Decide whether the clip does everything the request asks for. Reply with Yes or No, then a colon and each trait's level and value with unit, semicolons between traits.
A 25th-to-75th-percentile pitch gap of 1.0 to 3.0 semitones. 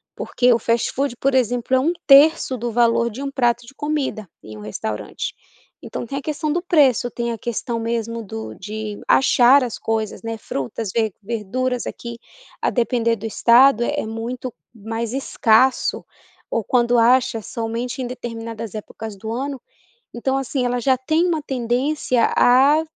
Yes: average, 2.7 semitones